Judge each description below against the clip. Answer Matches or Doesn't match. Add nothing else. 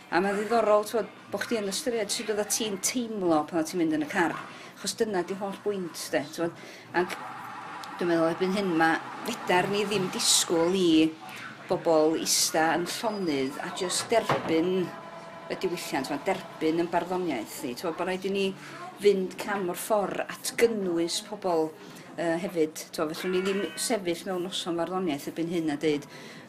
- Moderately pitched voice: Matches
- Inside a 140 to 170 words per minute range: Matches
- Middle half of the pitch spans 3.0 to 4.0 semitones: Matches